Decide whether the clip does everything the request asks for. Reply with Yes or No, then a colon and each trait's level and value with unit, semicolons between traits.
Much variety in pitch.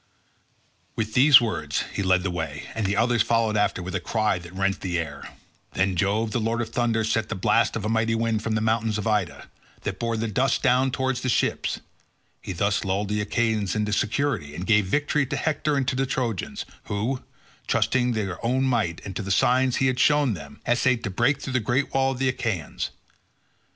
No: average, 3.9 semitones